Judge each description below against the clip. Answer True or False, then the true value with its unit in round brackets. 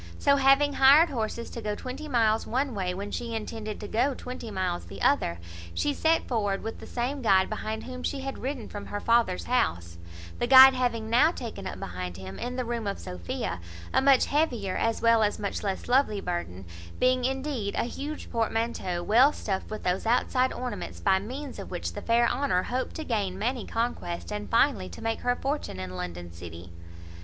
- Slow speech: False (200 wpm)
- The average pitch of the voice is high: True (230 Hz)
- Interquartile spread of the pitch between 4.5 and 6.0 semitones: True (4.8 semitones)